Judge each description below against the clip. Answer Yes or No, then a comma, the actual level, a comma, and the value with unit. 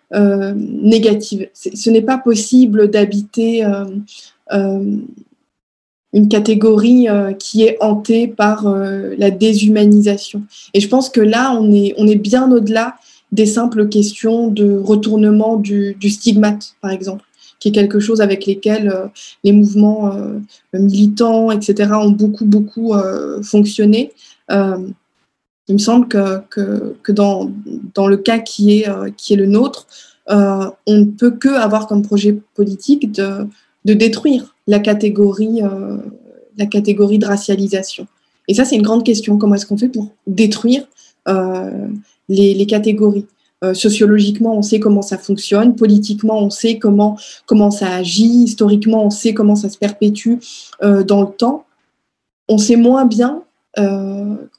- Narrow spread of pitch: Yes, narrow, 1.8 semitones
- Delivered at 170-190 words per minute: No, average, 155 wpm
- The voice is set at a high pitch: Yes, high, 210 Hz